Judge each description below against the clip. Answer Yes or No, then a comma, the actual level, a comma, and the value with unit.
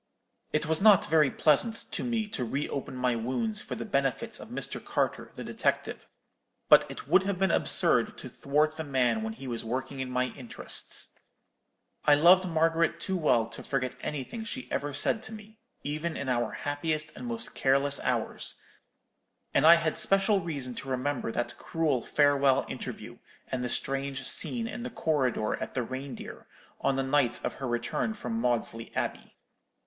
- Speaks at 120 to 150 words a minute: No, average, 175 wpm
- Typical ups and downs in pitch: Yes, average, 4.7 semitones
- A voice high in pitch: No, medium, 145 Hz